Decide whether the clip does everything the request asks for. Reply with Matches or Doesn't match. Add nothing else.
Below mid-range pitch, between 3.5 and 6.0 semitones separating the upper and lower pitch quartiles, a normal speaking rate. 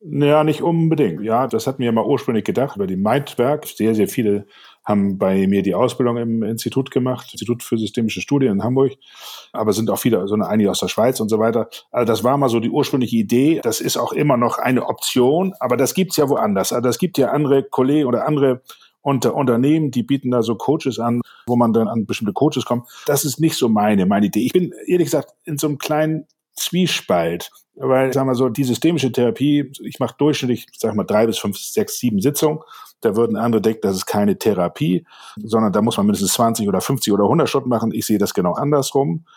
Doesn't match